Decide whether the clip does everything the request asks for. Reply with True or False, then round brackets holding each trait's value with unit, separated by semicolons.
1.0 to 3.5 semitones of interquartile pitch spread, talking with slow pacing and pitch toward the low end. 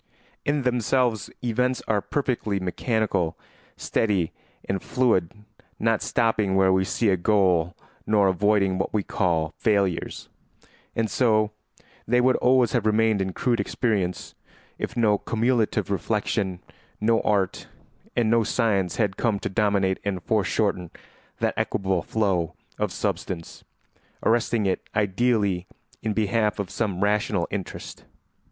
True (3.2 semitones; 130 wpm; 105 Hz)